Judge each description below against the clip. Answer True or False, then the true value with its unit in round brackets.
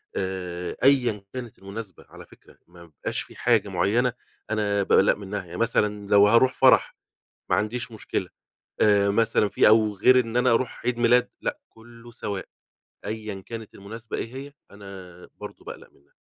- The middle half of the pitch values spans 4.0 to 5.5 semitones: False (3.0 semitones)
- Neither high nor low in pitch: False (105 Hz)